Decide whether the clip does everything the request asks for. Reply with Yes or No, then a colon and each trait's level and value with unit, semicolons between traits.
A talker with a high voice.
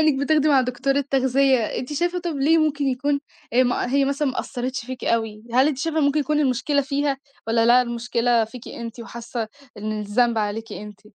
Yes: very high, 260 Hz